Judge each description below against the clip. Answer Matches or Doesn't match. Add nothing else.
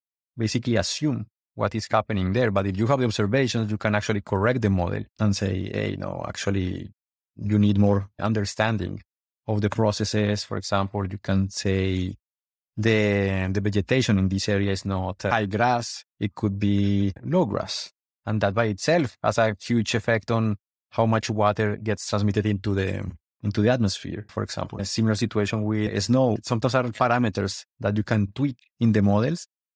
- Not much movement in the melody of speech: Matches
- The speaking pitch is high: Doesn't match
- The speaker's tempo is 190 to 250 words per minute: Doesn't match